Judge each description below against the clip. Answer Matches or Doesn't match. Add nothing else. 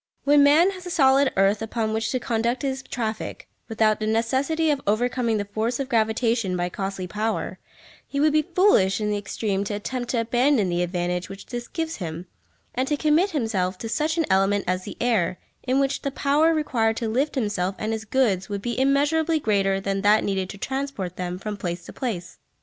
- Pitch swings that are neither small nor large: Doesn't match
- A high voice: Matches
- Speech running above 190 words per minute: Matches